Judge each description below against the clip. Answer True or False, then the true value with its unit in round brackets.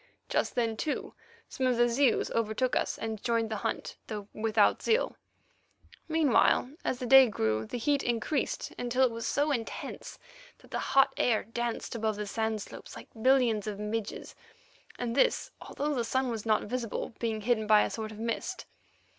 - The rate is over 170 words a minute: True (180 wpm)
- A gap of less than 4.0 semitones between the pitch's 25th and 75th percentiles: True (2.8 semitones)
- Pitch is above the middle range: True (230 Hz)